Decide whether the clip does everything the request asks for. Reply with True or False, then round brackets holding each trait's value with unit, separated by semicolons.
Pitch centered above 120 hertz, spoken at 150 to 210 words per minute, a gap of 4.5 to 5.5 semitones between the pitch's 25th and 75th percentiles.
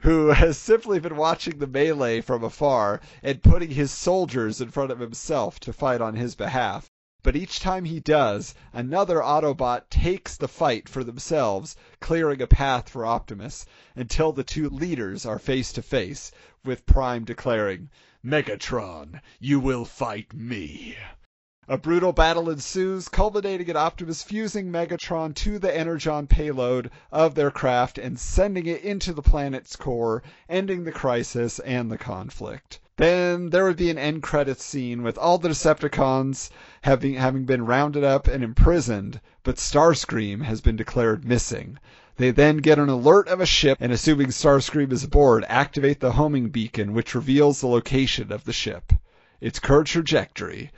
True (140 Hz; 160 wpm; 4.8 semitones)